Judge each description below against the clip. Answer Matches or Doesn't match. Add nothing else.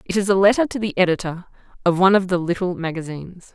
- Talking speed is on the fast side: Matches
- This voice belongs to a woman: Matches